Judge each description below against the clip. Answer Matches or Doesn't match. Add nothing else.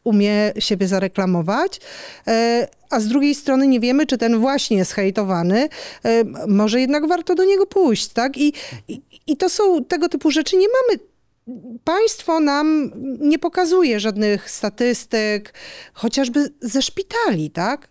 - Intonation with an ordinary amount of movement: Doesn't match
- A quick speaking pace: Doesn't match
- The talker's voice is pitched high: Matches